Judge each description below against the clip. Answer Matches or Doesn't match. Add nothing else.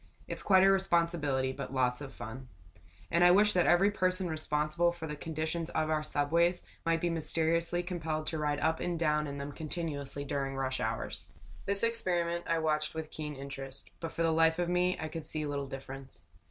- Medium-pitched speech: Matches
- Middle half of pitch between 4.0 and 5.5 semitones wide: Doesn't match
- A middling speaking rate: Matches